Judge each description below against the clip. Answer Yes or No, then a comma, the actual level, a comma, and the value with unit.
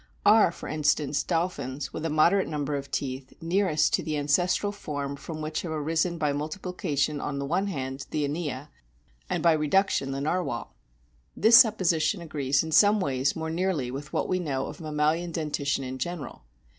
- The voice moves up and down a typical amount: Yes, average, 3.6 semitones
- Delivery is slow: No, average, 175 wpm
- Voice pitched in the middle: Yes, medium, 155 Hz